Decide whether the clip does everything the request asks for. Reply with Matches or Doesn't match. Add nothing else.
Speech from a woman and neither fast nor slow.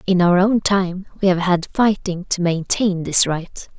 Matches